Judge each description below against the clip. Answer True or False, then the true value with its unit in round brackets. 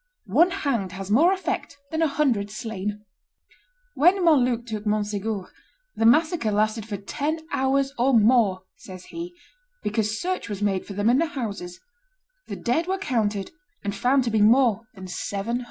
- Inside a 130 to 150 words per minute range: False (170 wpm)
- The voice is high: True (225 Hz)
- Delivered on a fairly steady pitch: False (5.2 semitones)